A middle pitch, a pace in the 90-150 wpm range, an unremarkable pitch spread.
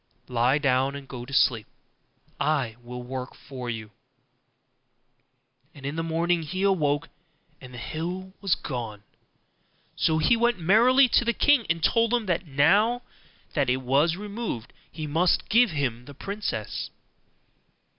No: medium, 155 Hz; average, 145 wpm; wide, 7.2 semitones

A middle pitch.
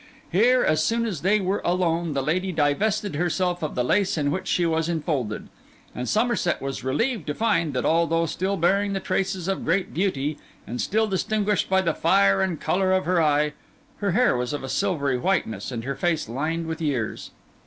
Yes: medium, 170 Hz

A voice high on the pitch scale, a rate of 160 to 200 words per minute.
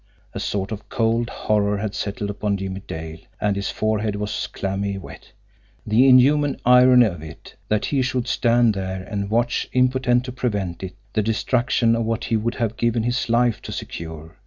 No: low, 110 Hz; average, 180 wpm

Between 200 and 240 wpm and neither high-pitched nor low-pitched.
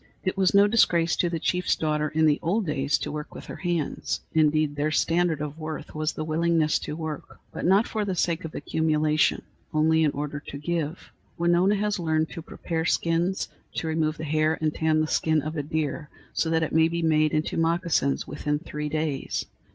Yes: fast, 205 wpm; medium, 160 Hz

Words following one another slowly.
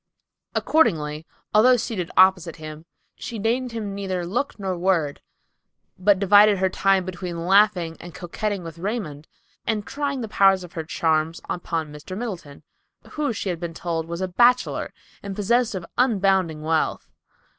No: average, 155 wpm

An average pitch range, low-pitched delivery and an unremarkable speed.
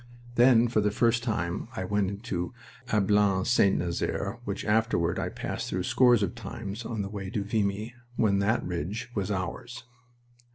Yes: average, 3.2 semitones; low, 105 Hz; average, 165 wpm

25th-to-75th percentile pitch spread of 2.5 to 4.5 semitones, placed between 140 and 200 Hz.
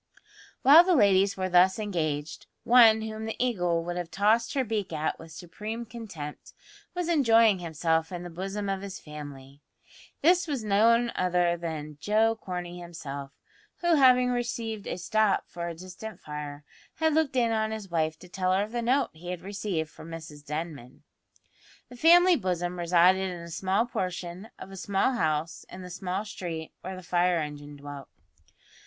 No: average, 4.9 semitones; medium, 185 Hz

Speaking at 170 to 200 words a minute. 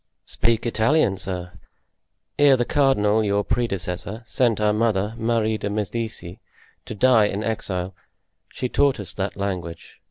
No: slow, 135 wpm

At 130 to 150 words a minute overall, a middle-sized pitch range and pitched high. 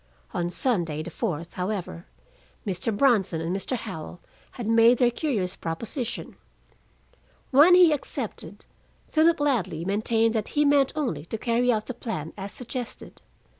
No: average, 140 wpm; wide, 6.0 semitones; high, 225 Hz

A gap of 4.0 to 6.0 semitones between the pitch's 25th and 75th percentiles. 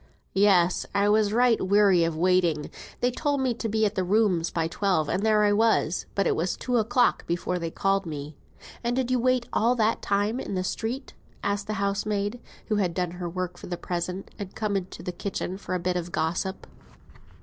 No: average, 3.5 semitones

